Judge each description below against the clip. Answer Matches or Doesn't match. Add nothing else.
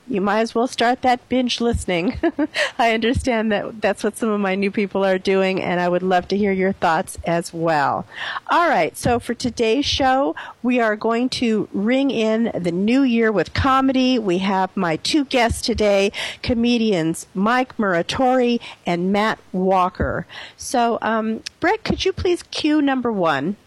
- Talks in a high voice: Matches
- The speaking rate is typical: Matches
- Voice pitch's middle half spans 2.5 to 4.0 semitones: Doesn't match